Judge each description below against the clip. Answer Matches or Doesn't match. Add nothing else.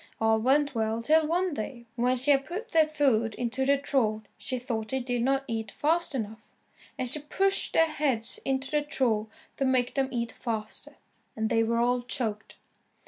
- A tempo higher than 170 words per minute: Matches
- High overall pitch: Matches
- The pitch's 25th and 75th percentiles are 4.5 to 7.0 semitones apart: Doesn't match